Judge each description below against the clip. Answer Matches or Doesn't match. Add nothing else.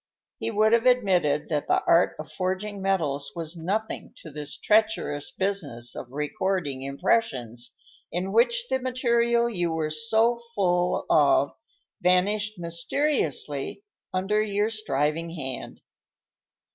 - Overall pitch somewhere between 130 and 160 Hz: Doesn't match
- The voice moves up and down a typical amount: Doesn't match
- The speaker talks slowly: Matches